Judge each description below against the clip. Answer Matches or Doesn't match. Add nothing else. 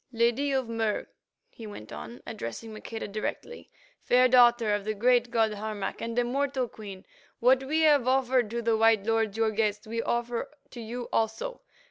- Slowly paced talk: Doesn't match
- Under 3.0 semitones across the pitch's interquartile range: Matches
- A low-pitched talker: Doesn't match